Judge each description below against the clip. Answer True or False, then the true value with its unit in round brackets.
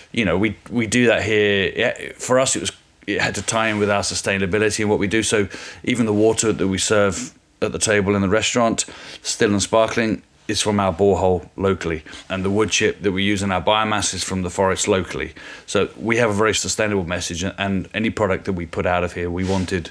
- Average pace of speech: False (230 wpm)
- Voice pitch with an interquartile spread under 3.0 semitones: True (2.4 semitones)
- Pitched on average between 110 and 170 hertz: False (100 Hz)